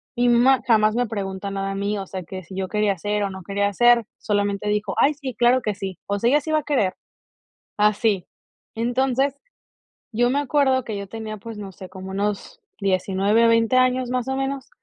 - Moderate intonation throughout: Yes, average, 4.1 semitones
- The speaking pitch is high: Yes, high, 215 Hz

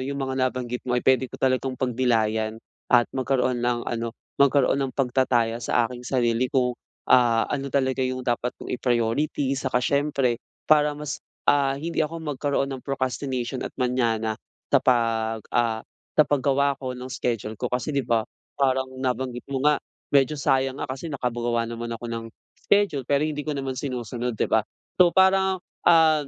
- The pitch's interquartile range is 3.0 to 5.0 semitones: No, narrow, 2.6 semitones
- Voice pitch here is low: Yes, low, 130 Hz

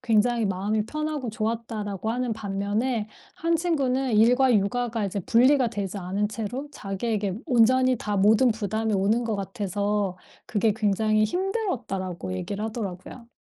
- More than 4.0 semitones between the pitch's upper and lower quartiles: No, average, 3.4 semitones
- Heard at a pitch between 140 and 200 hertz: No, high, 220 Hz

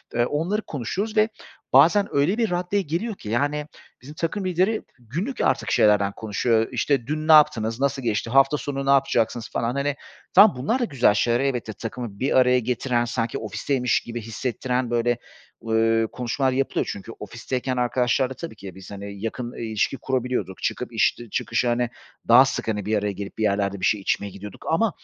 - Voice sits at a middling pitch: No, low, 125 Hz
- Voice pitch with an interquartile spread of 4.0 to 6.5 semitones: Yes, average, 4.3 semitones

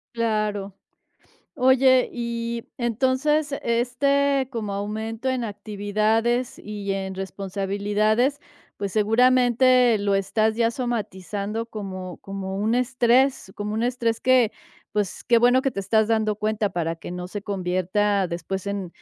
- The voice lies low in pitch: No, high, 220 Hz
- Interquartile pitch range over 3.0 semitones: Yes, average, 3.5 semitones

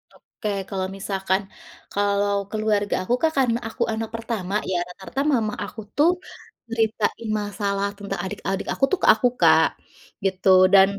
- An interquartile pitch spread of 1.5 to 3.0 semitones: Yes, narrow, 2.4 semitones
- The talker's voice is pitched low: No, high, 205 Hz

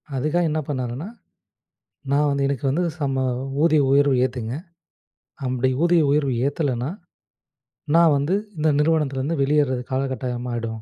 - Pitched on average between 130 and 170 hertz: Yes, medium, 140 Hz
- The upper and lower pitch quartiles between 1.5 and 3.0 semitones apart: Yes, average, 2.7 semitones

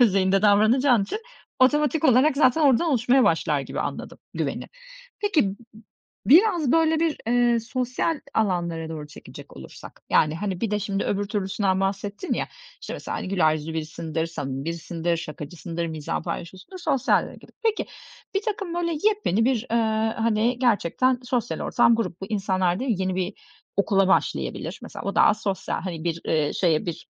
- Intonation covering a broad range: Yes, wide, 6.8 semitones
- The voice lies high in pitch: Yes, high, 205 Hz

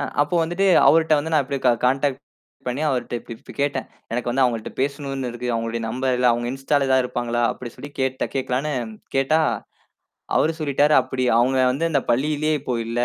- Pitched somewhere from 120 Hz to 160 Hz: Yes, low, 135 Hz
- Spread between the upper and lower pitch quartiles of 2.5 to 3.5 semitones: Yes, average, 2.8 semitones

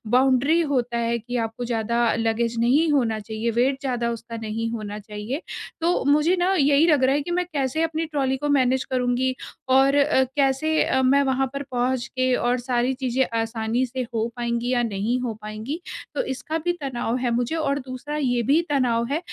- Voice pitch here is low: No, very high, 255 Hz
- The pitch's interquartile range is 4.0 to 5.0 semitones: No, average, 3.0 semitones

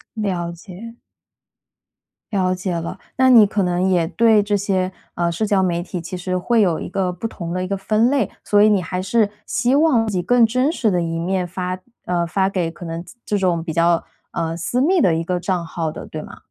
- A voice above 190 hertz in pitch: No, medium, 185 Hz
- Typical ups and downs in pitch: Yes, average, 3.6 semitones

